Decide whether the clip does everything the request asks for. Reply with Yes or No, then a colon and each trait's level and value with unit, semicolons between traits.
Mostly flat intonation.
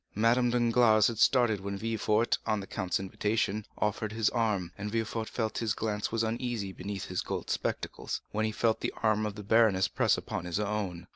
Yes: narrow, 2.1 semitones